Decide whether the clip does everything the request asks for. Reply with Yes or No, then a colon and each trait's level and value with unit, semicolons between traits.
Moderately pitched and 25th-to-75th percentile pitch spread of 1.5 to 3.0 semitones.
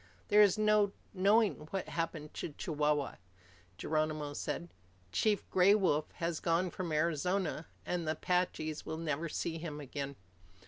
No: medium, 165 Hz; average, 3.5 semitones